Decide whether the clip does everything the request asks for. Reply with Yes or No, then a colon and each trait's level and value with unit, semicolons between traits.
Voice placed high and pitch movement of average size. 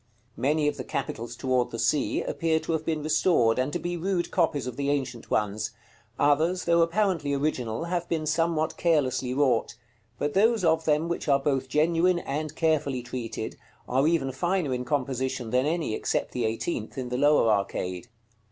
No: medium, 145 Hz; average, 4.5 semitones